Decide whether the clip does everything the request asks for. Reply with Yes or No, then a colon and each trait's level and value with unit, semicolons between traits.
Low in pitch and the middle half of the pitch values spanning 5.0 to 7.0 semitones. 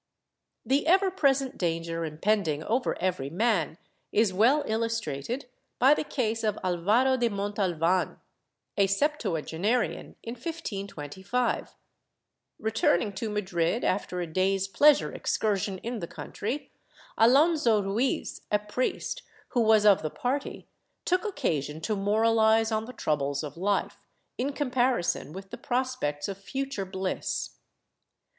No: high, 210 Hz; average, 5.3 semitones